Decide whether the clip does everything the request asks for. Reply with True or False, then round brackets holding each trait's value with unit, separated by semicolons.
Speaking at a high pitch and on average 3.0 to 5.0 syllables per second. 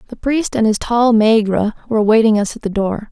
False (220 Hz; 6.1 syllables/s)